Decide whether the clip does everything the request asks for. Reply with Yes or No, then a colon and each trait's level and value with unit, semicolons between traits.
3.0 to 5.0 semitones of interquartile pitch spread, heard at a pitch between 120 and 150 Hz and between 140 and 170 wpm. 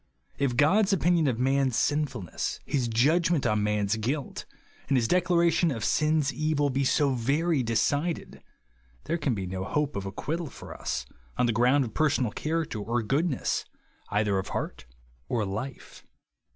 No: wide, 5.5 semitones; low, 135 Hz; average, 165 wpm